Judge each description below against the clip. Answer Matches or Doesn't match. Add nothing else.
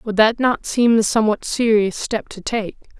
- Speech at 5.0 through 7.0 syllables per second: Doesn't match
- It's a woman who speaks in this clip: Matches